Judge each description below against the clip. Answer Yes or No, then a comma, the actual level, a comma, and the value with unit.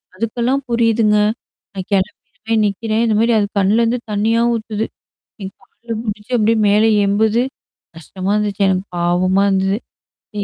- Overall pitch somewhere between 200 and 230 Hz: Yes, high, 210 Hz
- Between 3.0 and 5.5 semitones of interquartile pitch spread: No, narrow, 2.5 semitones